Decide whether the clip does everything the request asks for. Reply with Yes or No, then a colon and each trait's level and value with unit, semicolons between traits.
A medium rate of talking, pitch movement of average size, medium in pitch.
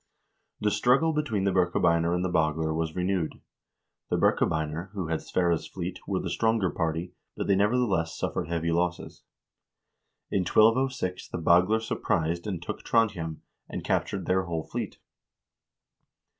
No: average, 145 wpm; average, 3.8 semitones; very low, 90 Hz